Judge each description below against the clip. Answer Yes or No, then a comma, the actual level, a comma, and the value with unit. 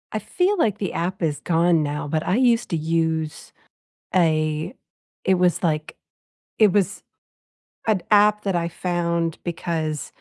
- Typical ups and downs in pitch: Yes, average, 3.6 semitones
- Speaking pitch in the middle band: Yes, medium, 170 Hz